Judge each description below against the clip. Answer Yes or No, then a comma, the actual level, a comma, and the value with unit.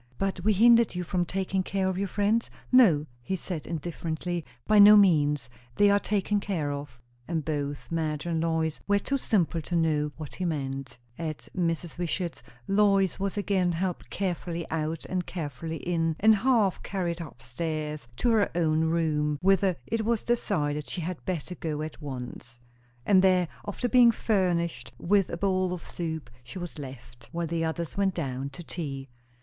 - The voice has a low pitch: No, medium, 170 Hz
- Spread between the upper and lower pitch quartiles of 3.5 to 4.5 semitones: Yes, average, 4.0 semitones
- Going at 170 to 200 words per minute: Yes, average, 175 wpm